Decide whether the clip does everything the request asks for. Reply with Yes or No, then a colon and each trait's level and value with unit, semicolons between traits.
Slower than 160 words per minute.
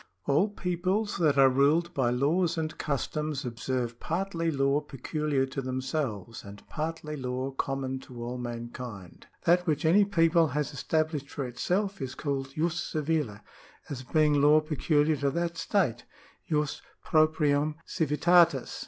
Yes: average, 145 wpm